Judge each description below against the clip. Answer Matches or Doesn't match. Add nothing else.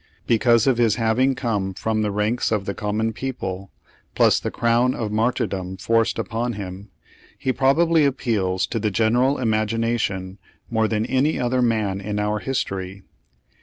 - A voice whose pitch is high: Doesn't match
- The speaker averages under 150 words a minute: Doesn't match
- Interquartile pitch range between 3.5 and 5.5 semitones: Doesn't match